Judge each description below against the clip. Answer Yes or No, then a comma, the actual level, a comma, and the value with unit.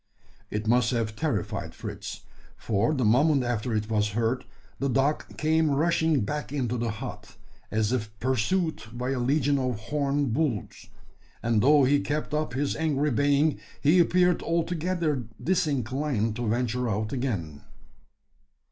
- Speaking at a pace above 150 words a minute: No, average, 145 wpm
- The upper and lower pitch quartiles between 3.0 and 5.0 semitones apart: Yes, average, 4.7 semitones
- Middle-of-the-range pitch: No, low, 130 Hz